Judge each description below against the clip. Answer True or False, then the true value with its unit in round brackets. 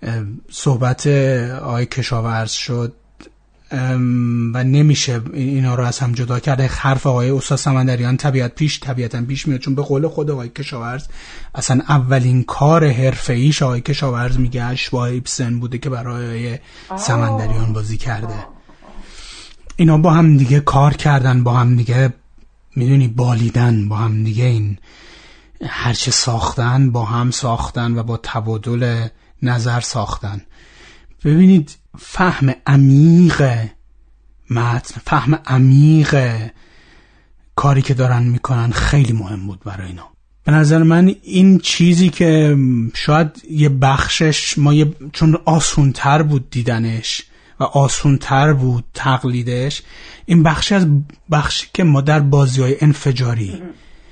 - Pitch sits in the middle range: False (130 Hz)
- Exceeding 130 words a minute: False (125 wpm)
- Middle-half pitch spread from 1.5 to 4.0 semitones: True (3.3 semitones)